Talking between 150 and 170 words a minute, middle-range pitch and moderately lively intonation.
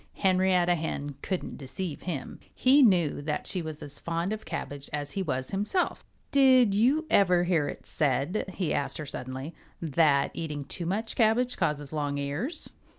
No: average, 165 wpm; medium, 170 Hz; wide, 5.7 semitones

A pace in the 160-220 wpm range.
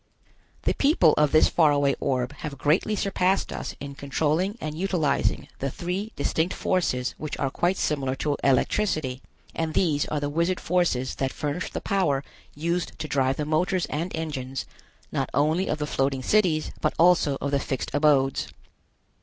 Yes: average, 170 wpm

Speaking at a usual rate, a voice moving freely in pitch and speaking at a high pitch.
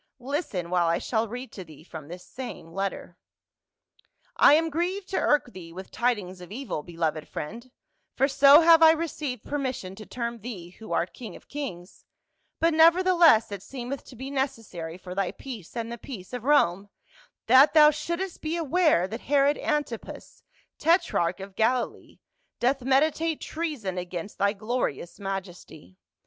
Yes: average, 175 wpm; wide, 7.9 semitones; high, 240 Hz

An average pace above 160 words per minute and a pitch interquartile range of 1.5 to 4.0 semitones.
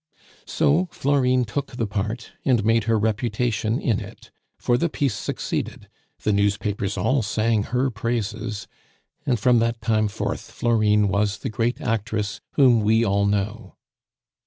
No: average, 145 wpm; narrow, 2.6 semitones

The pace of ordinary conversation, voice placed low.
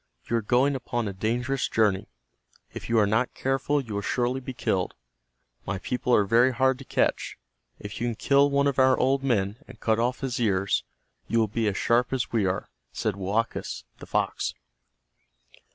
Yes: average, 190 wpm; low, 120 Hz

